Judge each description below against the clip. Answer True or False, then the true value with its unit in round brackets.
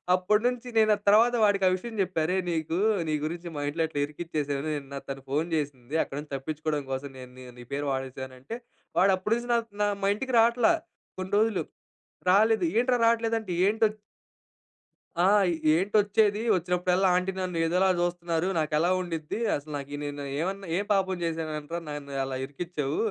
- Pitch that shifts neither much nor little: False (5.8 semitones)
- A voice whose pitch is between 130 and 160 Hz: False (175 Hz)